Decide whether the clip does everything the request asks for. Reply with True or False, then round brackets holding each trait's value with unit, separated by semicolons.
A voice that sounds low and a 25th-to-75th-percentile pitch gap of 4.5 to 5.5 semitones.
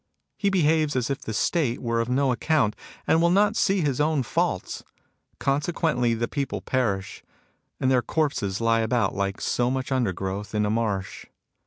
True (125 Hz; 5.1 semitones)